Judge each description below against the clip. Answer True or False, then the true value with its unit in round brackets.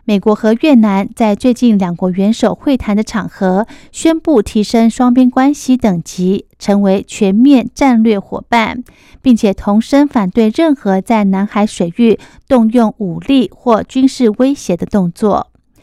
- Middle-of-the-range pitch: False (220 Hz)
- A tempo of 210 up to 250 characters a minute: True (225 characters per minute)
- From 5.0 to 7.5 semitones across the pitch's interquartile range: False (3.8 semitones)